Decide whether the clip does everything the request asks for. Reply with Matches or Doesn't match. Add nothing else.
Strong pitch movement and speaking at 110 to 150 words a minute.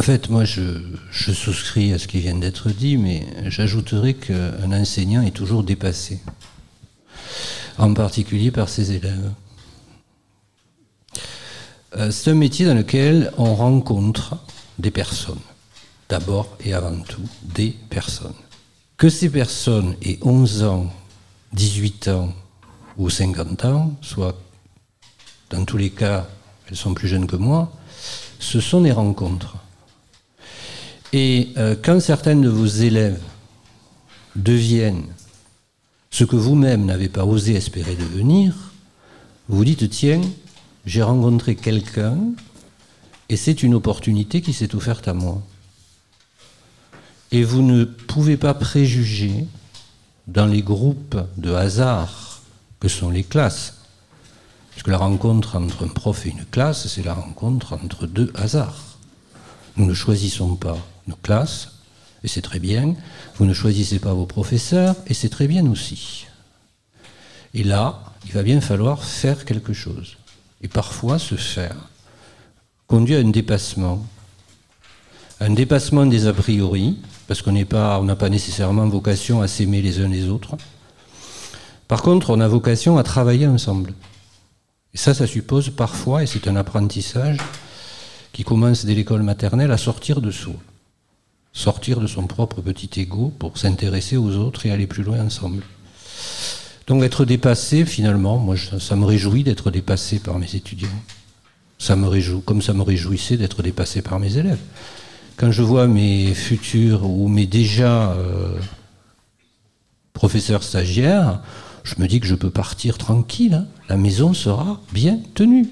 Doesn't match